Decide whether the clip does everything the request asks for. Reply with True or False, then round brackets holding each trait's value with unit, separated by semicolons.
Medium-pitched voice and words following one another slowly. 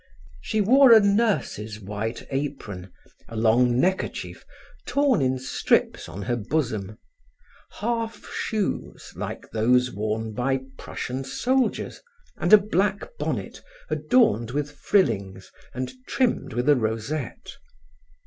False (130 Hz; 115 wpm)